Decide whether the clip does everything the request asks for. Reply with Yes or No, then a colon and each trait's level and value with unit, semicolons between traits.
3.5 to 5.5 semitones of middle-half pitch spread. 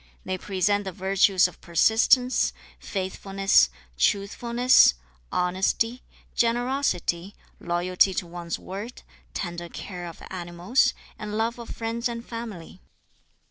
Yes: average, 4.5 semitones